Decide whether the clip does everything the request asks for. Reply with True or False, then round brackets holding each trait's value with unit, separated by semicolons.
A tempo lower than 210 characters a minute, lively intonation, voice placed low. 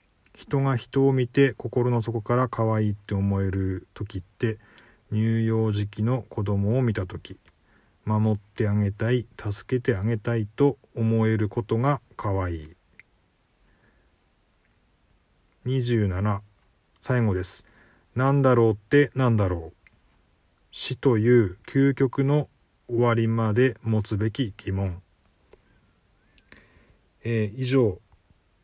False (200 characters per minute; 4.0 semitones; 110 Hz)